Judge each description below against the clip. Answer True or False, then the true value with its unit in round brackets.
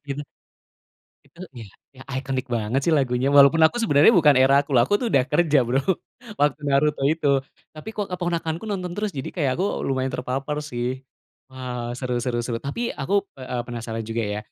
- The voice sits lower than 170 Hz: True (135 Hz)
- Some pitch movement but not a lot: True (4.0 semitones)